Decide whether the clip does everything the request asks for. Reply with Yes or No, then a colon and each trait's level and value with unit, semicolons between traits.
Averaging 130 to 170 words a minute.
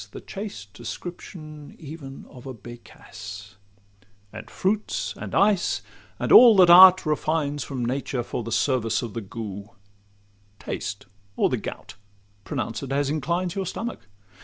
Yes: slow, 135 wpm